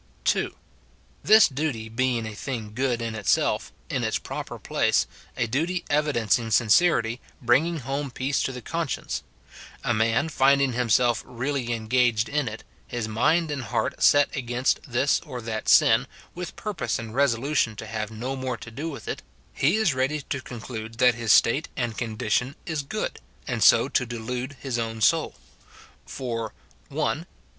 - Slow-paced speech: No, average, 170 wpm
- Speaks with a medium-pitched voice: No, low, 125 Hz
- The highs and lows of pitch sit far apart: No, average, 3.6 semitones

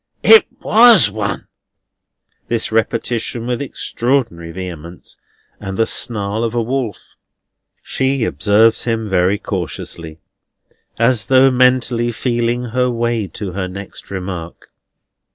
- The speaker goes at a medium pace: No, slow, 115 wpm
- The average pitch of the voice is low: Yes, low, 115 Hz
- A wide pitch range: No, average, 4.0 semitones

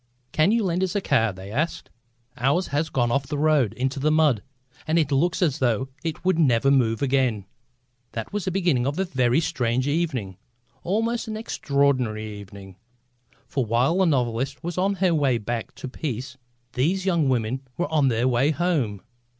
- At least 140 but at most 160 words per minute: No, average, 185 wpm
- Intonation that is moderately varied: No, wide, 5.8 semitones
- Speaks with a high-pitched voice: No, medium, 140 Hz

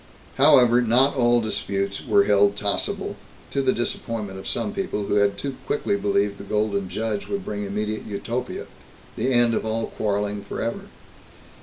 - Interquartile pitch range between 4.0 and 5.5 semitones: No, average, 3.1 semitones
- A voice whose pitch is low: Yes, low, 105 Hz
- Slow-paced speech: No, average, 160 wpm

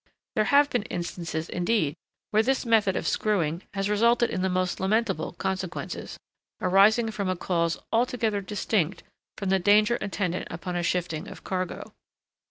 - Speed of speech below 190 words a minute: Yes, average, 155 wpm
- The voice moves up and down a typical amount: Yes, average, 3.5 semitones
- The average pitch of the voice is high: Yes, high, 195 Hz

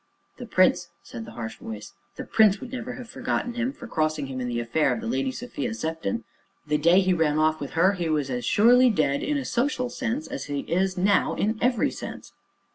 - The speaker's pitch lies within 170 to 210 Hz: Yes, medium, 185 Hz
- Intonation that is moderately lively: No, wide, 8.5 semitones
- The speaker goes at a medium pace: No, fast, 220 wpm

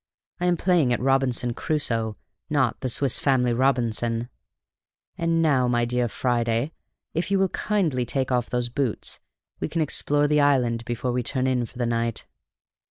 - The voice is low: Yes, low, 125 Hz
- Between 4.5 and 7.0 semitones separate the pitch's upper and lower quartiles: No, average, 3.5 semitones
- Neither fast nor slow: Yes, average, 165 wpm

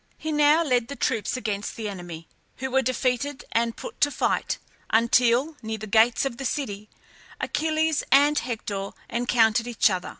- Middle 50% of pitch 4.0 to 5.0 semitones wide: Yes, average, 4.3 semitones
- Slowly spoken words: No, average, 165 wpm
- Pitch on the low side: No, high, 240 Hz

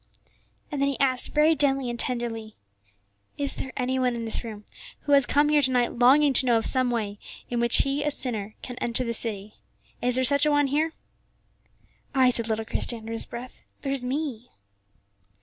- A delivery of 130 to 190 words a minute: No, average, 200 wpm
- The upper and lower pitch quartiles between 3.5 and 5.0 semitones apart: No, average, 3.1 semitones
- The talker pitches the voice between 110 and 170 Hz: No, very high, 250 Hz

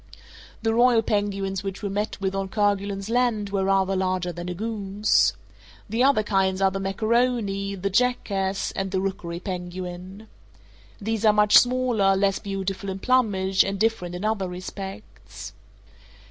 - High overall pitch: Yes, high, 195 Hz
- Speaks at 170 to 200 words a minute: No, average, 150 wpm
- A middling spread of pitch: No, narrow, 2.1 semitones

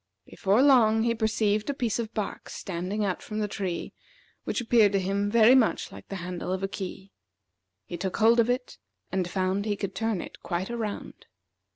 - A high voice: Yes, high, 205 Hz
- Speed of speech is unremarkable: Yes, average, 195 wpm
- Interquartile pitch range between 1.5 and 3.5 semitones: Yes, average, 2.9 semitones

